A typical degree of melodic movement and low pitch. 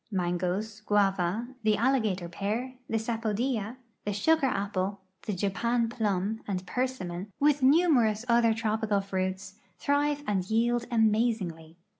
No: average, 3.5 semitones; high, 215 Hz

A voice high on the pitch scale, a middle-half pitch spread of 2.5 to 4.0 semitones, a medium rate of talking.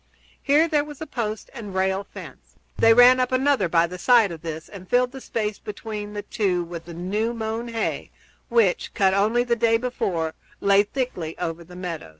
No: high, 210 Hz; average, 5.1 semitones; average, 195 wpm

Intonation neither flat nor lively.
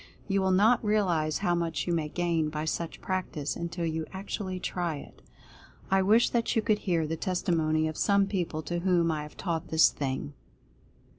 Yes: average, 3.3 semitones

